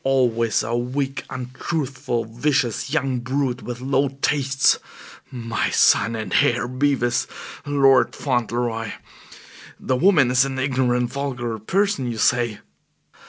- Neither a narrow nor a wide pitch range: No, narrow, 2.2 semitones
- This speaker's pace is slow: Yes, slow, 115 wpm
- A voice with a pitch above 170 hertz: No, low, 125 Hz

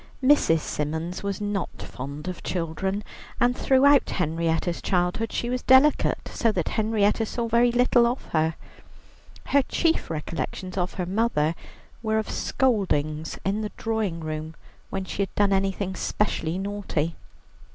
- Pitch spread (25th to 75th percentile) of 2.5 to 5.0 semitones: No, wide, 5.5 semitones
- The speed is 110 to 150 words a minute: Yes, average, 140 wpm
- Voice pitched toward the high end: Yes, high, 195 Hz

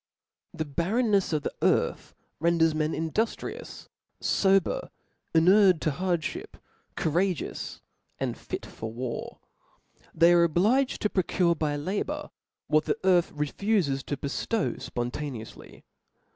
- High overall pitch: No, medium, 170 Hz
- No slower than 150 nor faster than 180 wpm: No, slow, 135 wpm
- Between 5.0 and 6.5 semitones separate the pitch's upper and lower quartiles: No, average, 4.5 semitones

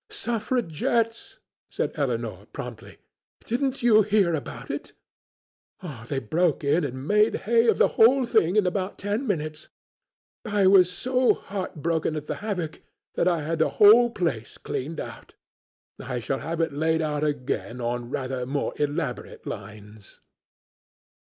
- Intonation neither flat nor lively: No, wide, 6.7 semitones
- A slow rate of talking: No, average, 145 wpm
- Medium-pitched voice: Yes, medium, 170 Hz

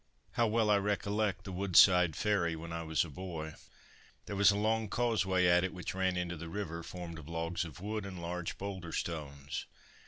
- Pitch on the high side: No, very low, 90 Hz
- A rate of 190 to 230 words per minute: Yes, average, 195 wpm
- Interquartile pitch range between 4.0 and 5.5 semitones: No, average, 3.4 semitones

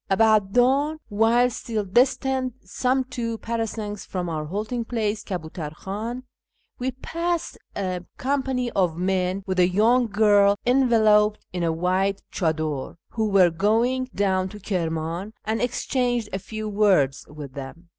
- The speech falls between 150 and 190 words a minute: No, average, 140 wpm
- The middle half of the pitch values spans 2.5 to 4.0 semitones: No, average, 4.8 semitones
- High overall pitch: Yes, high, 210 Hz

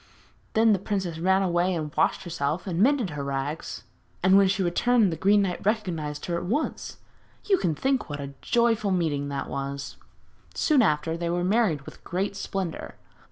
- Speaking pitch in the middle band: Yes, medium, 180 Hz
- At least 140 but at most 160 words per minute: No, average, 180 wpm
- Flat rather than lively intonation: No, average, 4.9 semitones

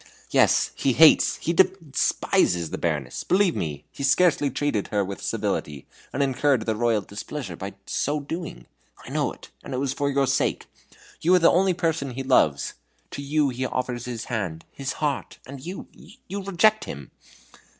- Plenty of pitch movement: Yes, wide, 6.9 semitones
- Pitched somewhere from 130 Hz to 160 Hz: Yes, low, 135 Hz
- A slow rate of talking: No, average, 175 wpm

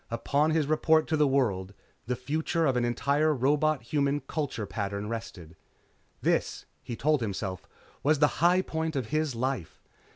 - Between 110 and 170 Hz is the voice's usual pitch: Yes, medium, 140 Hz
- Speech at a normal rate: Yes, average, 160 wpm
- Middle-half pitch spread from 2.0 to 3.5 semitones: No, average, 5.2 semitones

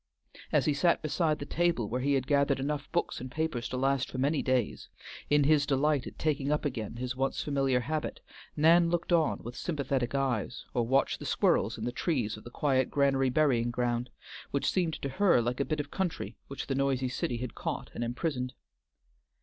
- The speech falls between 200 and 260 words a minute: Yes, fast, 205 wpm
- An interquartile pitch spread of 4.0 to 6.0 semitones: No, average, 3.1 semitones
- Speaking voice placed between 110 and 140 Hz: Yes, low, 135 Hz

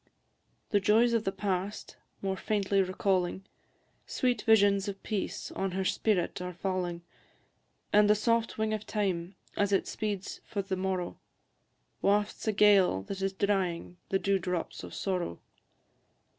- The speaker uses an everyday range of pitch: No, narrow, 2.0 semitones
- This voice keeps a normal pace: Yes, average, 145 wpm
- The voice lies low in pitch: No, high, 195 Hz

